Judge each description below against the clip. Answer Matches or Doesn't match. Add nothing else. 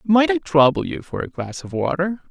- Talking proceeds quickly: Matches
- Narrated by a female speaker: Doesn't match